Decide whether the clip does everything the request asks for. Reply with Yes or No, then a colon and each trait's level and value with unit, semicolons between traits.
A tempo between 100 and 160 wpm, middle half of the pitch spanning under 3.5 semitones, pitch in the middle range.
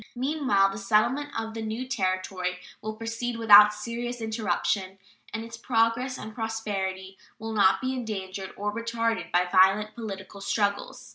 No: average, 145 wpm; average, 2.9 semitones; high, 215 Hz